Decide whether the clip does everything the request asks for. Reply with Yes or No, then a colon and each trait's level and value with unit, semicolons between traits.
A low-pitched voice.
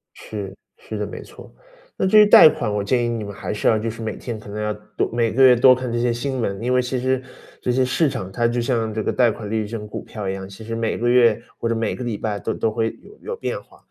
Yes: low, 115 Hz